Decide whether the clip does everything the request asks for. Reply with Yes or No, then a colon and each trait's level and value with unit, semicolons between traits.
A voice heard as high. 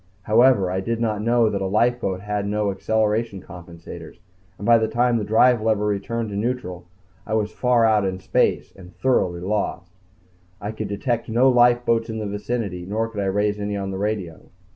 No: low, 105 Hz